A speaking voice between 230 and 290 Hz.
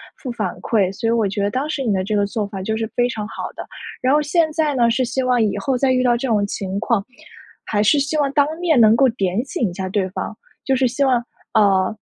Yes: high, 235 Hz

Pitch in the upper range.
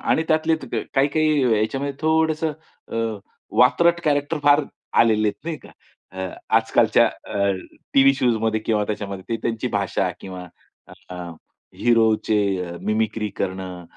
No: low, 115 Hz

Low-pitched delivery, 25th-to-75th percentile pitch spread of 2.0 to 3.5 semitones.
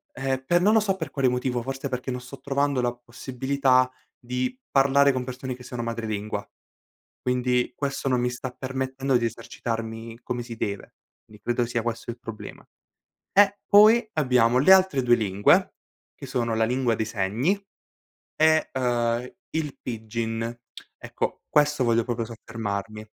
Yes: low, 125 Hz; average, 2.7 semitones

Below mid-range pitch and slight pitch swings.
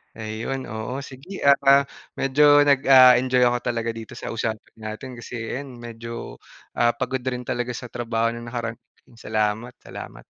Yes: low, 120 Hz; narrow, 2.2 semitones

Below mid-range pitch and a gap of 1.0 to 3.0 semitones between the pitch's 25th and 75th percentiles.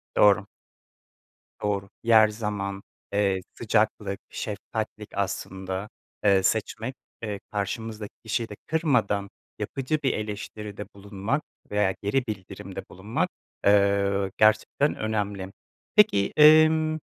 Yes: low, 105 Hz; narrow, 2.5 semitones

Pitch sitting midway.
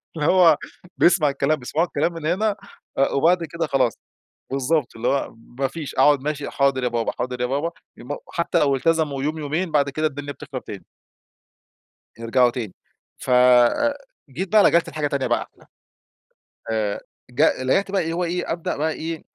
Yes: medium, 145 Hz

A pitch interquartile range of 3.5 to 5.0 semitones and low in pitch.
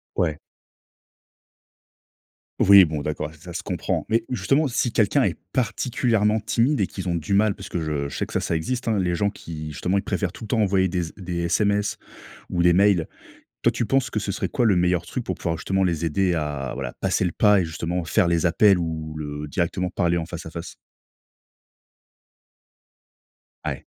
Yes: average, 3.9 semitones; very low, 90 Hz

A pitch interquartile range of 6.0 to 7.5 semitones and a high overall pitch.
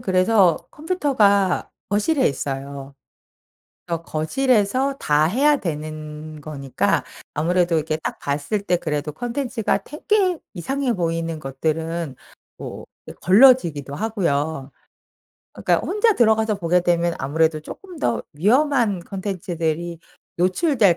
No: wide, 7.0 semitones; medium, 175 Hz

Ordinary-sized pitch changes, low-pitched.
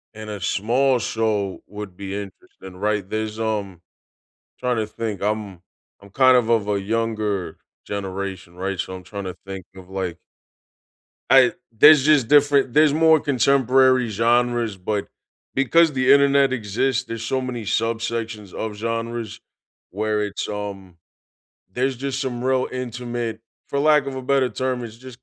Yes: average, 4.1 semitones; low, 115 Hz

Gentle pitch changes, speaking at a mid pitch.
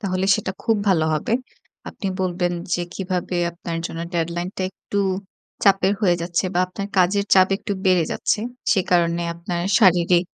Yes: narrow, 1.9 semitones; medium, 180 Hz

